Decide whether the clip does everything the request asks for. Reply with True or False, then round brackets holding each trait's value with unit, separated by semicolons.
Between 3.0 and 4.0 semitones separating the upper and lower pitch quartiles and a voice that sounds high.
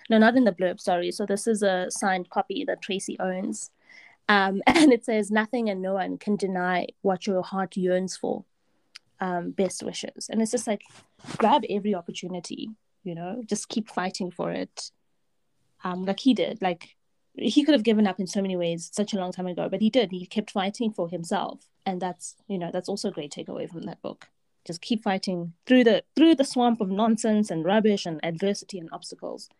True (3.3 semitones; 195 Hz)